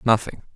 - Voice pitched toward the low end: Yes, low, 110 Hz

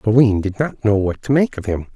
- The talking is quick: Yes, fast, 275 wpm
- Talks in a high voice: No, low, 110 Hz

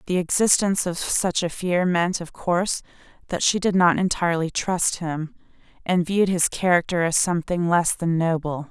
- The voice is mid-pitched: Yes, medium, 175 Hz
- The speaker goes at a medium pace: Yes, average, 170 wpm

